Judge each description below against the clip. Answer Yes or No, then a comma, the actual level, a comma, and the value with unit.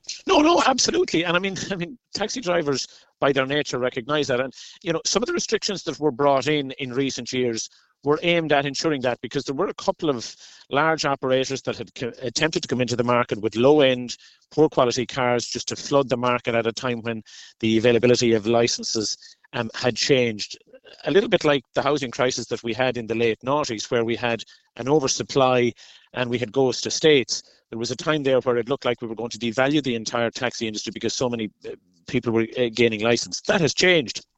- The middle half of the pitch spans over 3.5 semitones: Yes, average, 4.0 semitones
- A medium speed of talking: No, fast, 220 wpm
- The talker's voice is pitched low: Yes, low, 125 Hz